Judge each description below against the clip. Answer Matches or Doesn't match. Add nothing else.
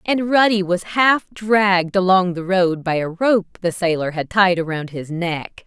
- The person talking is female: Matches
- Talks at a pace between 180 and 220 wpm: Matches